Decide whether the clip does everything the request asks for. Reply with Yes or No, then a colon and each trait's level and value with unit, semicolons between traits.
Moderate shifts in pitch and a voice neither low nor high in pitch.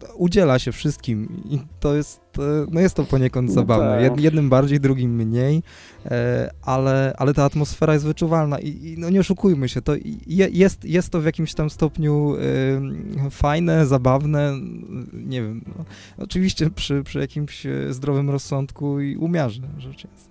Yes: average, 3.4 semitones; medium, 145 Hz